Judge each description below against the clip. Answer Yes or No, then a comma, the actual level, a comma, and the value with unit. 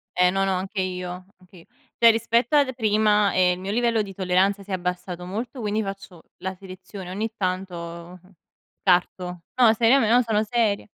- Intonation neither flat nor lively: Yes, average, 3.2 semitones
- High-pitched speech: Yes, high, 195 Hz